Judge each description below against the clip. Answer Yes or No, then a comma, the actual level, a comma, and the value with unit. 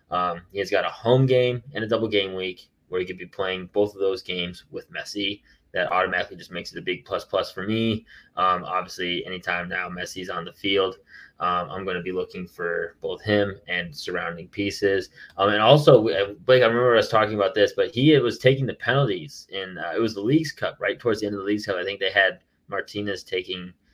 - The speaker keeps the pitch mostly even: No, average, 3.6 semitones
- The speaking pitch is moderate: No, low, 100 Hz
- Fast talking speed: Yes, fast, 230 wpm